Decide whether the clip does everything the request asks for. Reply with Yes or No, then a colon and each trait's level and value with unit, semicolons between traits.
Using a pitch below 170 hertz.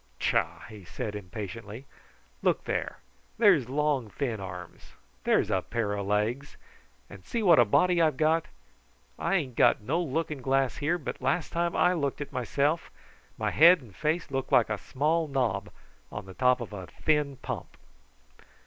Yes: low, 135 Hz